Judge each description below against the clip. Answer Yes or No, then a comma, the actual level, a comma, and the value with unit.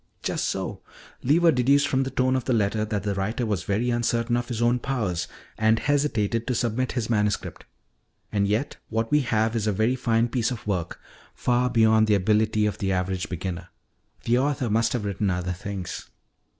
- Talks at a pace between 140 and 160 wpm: No, average, 190 wpm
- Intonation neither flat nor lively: Yes, average, 3.4 semitones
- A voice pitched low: Yes, low, 110 Hz